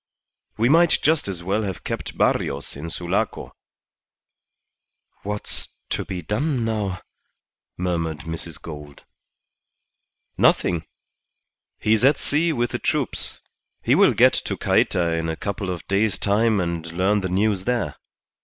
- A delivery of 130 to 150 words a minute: Yes, slow, 135 wpm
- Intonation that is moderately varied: Yes, average, 4.8 semitones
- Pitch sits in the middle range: No, very low, 95 Hz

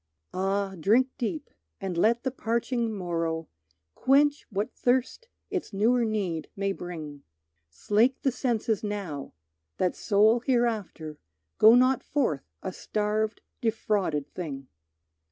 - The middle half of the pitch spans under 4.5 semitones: No, average, 5.1 semitones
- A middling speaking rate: No, slow, 120 wpm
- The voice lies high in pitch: Yes, high, 210 Hz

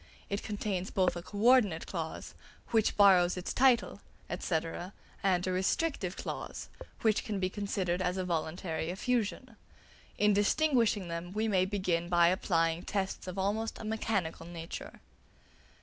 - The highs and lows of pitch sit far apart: No, average, 3.2 semitones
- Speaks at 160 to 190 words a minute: No, average, 145 wpm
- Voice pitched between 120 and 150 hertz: No, high, 190 Hz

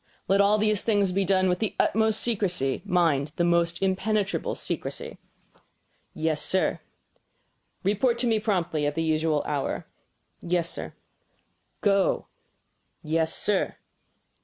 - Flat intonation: No, average, 4.2 semitones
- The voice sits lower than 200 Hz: Yes, medium, 185 Hz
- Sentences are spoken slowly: Yes, slow, 125 wpm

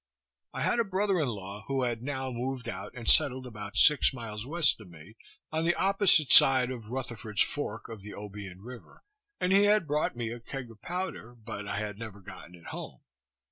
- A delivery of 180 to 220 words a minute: Yes, fast, 205 wpm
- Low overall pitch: Yes, low, 120 Hz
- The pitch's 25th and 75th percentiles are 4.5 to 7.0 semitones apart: Yes, wide, 5.5 semitones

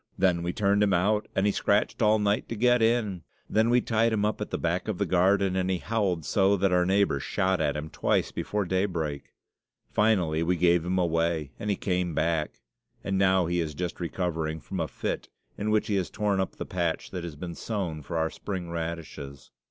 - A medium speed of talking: No, fast, 215 wpm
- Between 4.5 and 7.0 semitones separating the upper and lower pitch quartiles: No, average, 3.4 semitones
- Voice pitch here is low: Yes, very low, 90 Hz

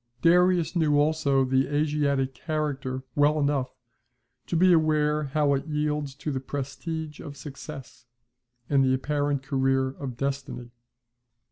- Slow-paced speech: Yes, slow, 130 wpm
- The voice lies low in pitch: No, medium, 145 Hz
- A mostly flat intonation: Yes, narrow, 2.2 semitones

